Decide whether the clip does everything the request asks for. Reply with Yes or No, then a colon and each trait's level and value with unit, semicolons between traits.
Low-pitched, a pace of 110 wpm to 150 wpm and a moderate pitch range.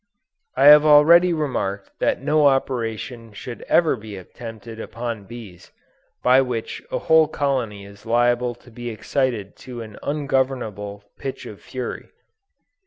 Yes: low, 120 Hz; slow, 135 wpm; average, 3.8 semitones